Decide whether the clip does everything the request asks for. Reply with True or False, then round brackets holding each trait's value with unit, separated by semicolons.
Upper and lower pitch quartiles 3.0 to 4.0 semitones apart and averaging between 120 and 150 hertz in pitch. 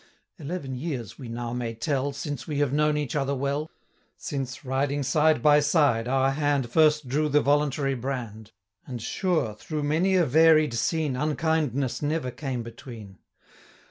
True (3.3 semitones; 140 Hz)